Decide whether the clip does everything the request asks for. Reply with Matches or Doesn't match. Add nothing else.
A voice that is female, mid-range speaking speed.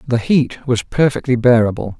Doesn't match